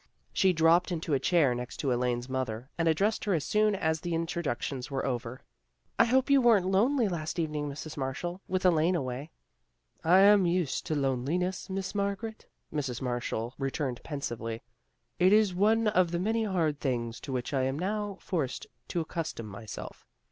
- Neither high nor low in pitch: Yes, medium, 160 Hz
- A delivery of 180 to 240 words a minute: Yes, average, 185 wpm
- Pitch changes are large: Yes, wide, 6.4 semitones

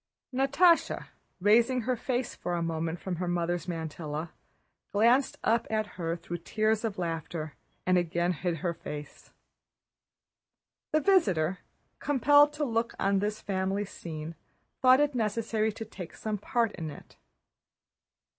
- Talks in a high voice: Yes, high, 200 Hz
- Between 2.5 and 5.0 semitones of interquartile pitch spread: No, wide, 5.5 semitones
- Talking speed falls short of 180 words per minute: Yes, average, 140 wpm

